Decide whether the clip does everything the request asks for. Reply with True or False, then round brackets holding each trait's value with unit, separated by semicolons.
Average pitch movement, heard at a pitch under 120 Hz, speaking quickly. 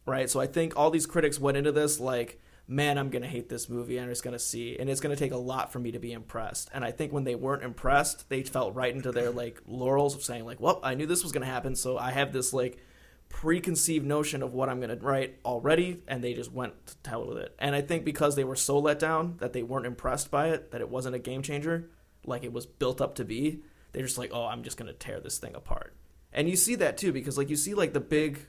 False (3.2 semitones; 135 Hz; 270 wpm)